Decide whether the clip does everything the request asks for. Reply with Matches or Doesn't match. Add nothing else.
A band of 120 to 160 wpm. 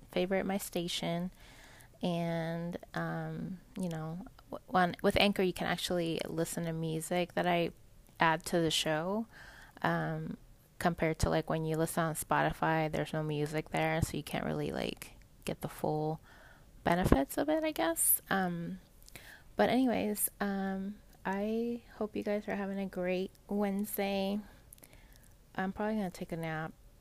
Matches